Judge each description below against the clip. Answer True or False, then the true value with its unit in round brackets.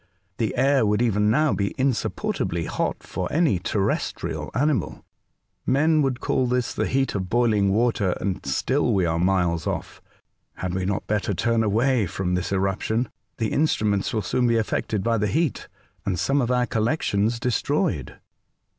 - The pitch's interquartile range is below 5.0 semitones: True (4.5 semitones)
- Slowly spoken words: False (165 wpm)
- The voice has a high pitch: False (110 Hz)